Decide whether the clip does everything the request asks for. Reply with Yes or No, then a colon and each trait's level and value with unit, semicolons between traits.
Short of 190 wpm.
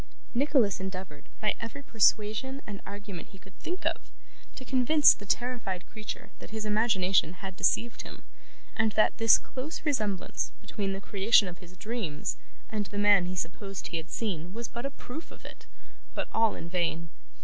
Yes: average, 175 wpm